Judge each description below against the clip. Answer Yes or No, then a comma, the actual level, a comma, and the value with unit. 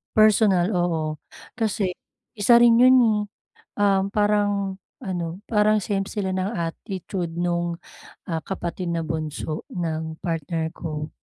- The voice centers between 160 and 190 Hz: Yes, medium, 185 Hz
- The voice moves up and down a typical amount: Yes, average, 3.9 semitones